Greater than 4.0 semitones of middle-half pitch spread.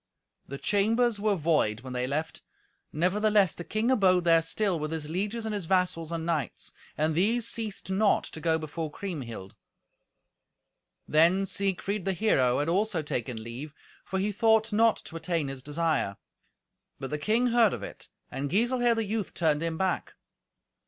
Yes: wide, 5.5 semitones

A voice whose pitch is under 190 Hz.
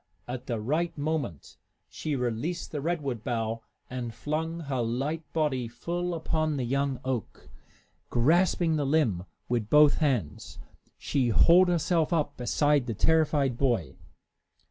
Yes: medium, 140 Hz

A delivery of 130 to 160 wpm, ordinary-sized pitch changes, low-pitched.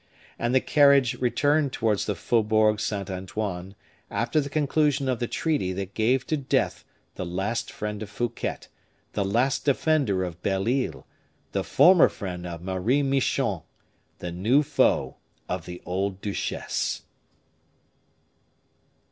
No: slow, 135 wpm; wide, 6.1 semitones; low, 110 Hz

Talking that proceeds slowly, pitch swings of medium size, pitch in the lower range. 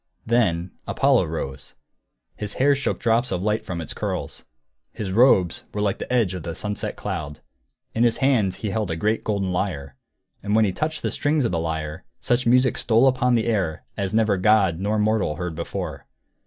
No: average, 190 wpm; average, 4.6 semitones; low, 105 Hz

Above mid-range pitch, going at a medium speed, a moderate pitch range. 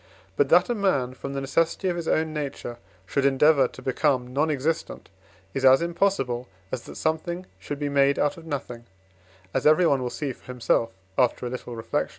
No: medium, 140 Hz; average, 190 wpm; average, 3.9 semitones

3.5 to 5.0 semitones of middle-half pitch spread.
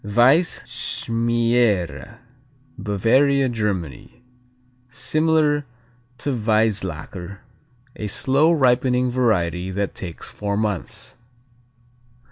Yes: average, 4.4 semitones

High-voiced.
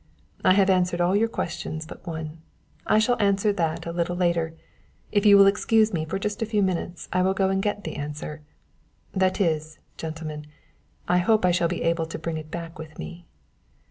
No: medium, 175 Hz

